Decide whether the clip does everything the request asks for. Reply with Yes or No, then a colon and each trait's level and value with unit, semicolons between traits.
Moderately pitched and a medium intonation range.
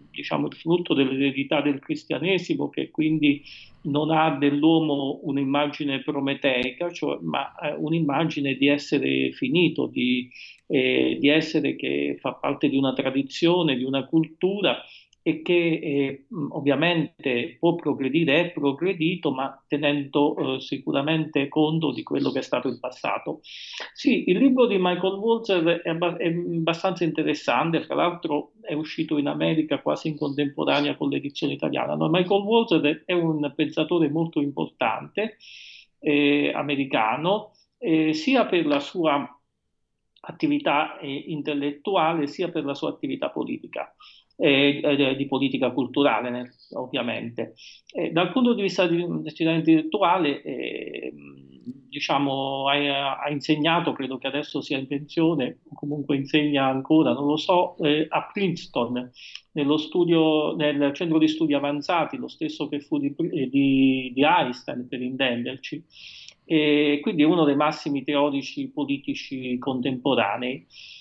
Yes: medium, 150 Hz; average, 3.0 semitones